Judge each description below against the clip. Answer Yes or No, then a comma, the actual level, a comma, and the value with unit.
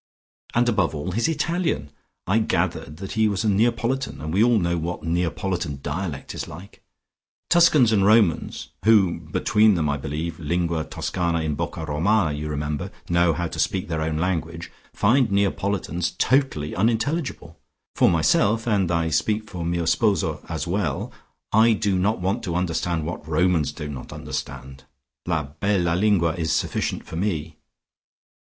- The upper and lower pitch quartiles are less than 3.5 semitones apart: No, average, 4.9 semitones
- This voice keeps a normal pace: Yes, average, 155 wpm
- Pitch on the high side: No, very low, 90 Hz